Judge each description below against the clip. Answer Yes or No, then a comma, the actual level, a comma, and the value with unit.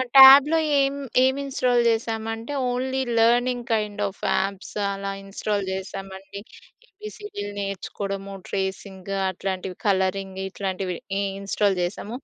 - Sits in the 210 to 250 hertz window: No, high, 200 Hz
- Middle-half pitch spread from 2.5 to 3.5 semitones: No, average, 3.9 semitones